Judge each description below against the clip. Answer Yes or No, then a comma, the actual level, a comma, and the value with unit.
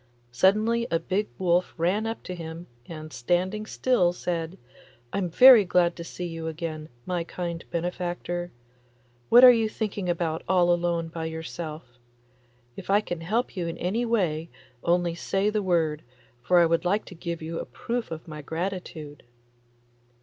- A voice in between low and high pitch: Yes, medium, 175 Hz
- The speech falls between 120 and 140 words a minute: No, average, 165 wpm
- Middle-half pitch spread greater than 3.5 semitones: No, average, 2.9 semitones